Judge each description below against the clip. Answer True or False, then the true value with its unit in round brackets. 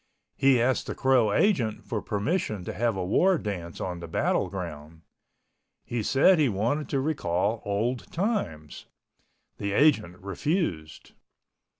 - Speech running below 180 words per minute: True (135 wpm)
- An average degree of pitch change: False (7.1 semitones)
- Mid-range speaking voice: False (110 Hz)